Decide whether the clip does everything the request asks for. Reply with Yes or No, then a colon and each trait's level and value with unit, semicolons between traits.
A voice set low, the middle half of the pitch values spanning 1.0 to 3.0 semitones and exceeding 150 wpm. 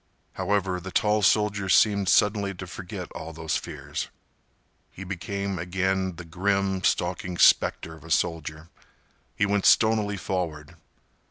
No: very low, 95 Hz; average, 2.7 semitones; slow, 135 wpm